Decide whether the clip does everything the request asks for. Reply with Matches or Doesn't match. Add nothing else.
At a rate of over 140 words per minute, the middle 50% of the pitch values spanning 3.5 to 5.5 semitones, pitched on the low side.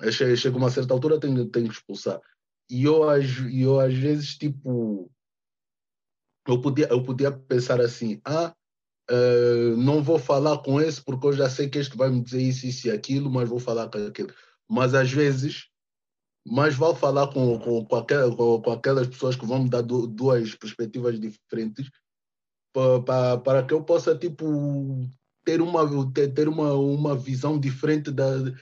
Doesn't match